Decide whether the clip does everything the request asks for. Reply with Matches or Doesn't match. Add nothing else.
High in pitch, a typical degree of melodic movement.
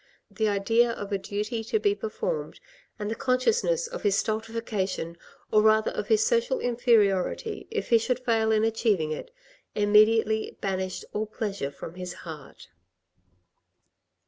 Matches